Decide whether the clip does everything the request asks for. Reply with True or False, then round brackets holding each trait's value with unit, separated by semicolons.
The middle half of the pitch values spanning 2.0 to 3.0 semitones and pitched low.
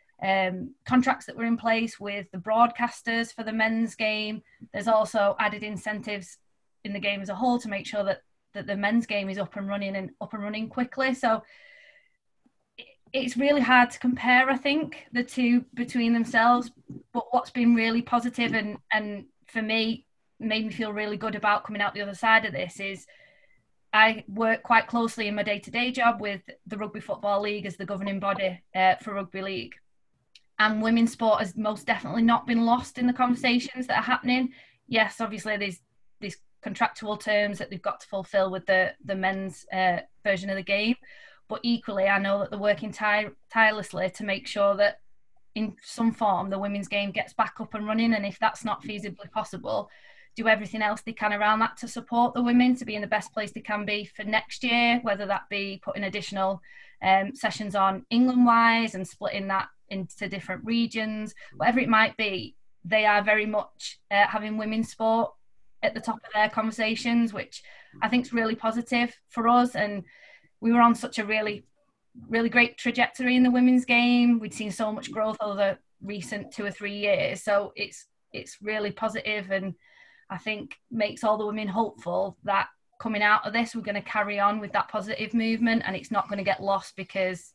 False (2.6 semitones; 215 Hz)